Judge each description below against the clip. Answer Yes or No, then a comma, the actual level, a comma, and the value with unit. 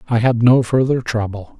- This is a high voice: No, low, 120 Hz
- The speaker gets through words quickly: No, average, 190 wpm